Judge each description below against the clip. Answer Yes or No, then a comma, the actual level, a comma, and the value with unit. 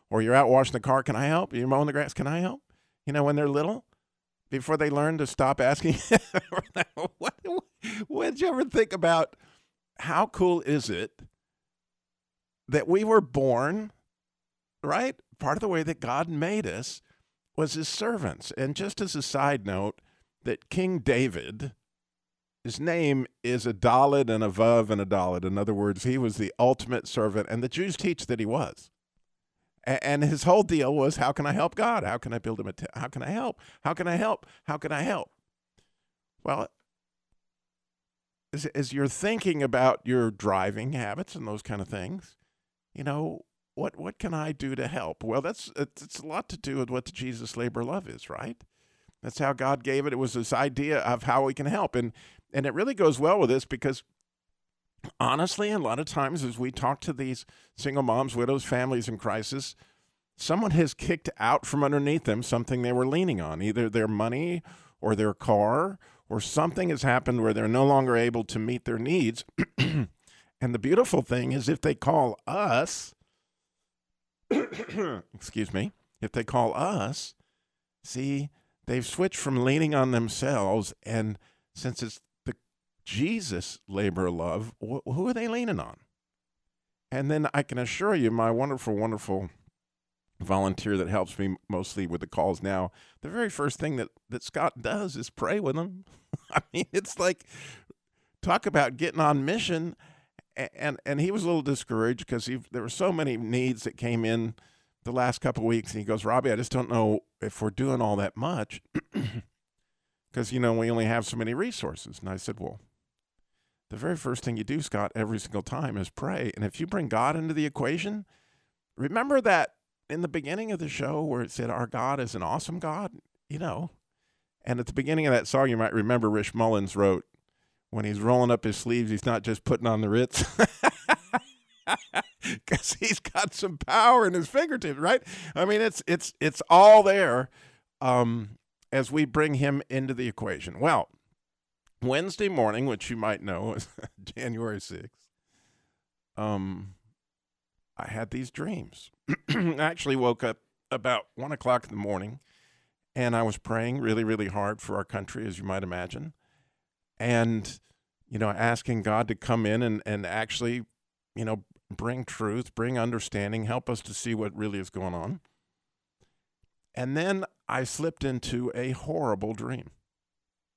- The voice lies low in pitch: Yes, low, 125 Hz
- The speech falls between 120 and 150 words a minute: No, average, 175 wpm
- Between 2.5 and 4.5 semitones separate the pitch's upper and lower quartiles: No, wide, 5.4 semitones